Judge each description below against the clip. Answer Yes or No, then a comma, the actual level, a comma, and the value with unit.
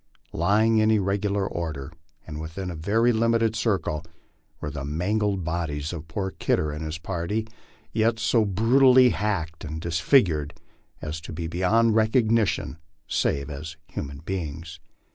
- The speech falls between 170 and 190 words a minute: No, average, 145 wpm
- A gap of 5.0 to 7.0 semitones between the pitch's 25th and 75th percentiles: Yes, wide, 5.6 semitones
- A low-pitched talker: Yes, very low, 90 Hz